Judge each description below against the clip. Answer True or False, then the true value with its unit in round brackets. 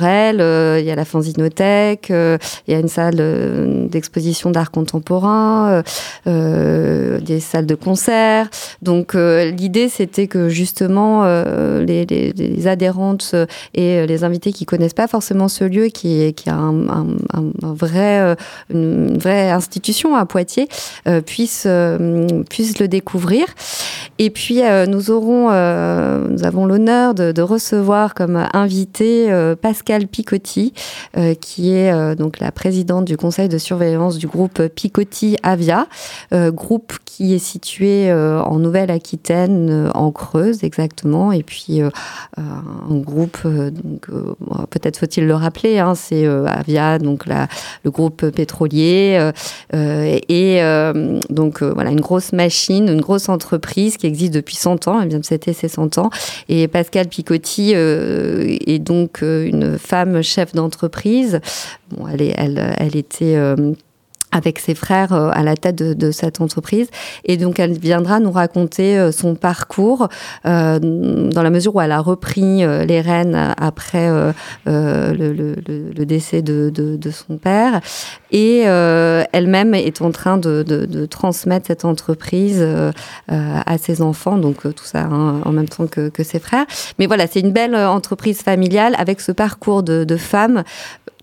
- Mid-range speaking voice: True (175 Hz)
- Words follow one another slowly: False (155 wpm)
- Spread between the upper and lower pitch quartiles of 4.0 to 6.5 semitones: False (3.6 semitones)